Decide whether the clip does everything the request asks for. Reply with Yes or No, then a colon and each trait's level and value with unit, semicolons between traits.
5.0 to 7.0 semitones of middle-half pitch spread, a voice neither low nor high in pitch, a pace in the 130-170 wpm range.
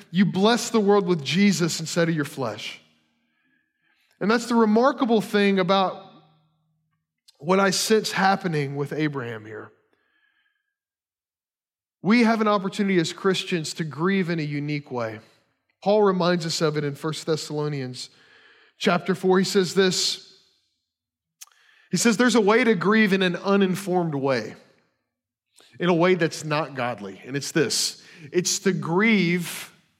Yes: average, 5.3 semitones; medium, 180 Hz; average, 140 wpm